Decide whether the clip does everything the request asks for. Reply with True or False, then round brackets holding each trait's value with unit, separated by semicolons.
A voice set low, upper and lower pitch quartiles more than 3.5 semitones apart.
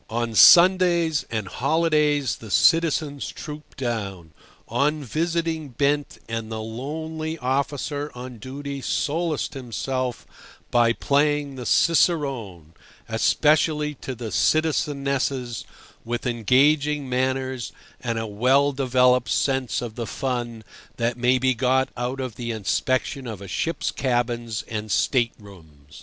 True (130 Hz; 3.9 semitones)